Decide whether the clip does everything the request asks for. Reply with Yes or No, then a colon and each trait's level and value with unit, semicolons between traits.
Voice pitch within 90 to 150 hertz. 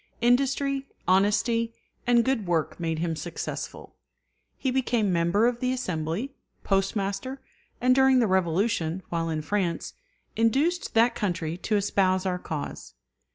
No: high, 205 Hz